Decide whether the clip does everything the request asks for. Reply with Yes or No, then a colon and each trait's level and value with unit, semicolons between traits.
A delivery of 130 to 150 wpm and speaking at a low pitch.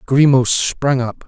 Yes: average, 140 wpm; low, 130 Hz